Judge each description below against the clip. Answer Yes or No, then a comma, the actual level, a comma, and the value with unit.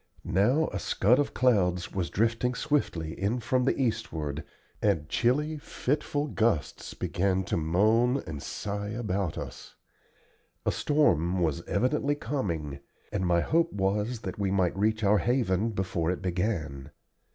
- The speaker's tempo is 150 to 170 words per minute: No, average, 140 wpm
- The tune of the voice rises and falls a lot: Yes, wide, 5.8 semitones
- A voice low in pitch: Yes, low, 100 Hz